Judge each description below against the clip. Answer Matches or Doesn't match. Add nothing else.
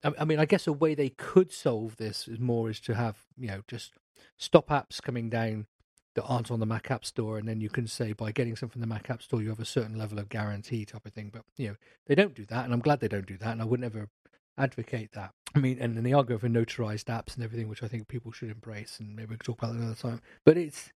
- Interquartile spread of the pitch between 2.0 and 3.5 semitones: Matches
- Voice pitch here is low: Matches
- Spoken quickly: Matches